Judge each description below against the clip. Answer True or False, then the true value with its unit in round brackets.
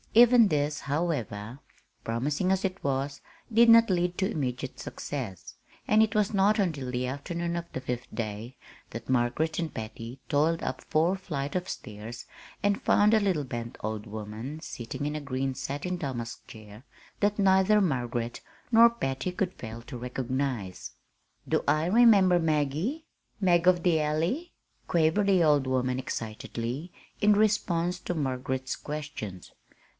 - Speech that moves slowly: False (150 wpm)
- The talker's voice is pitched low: False (150 Hz)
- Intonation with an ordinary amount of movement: False (6.6 semitones)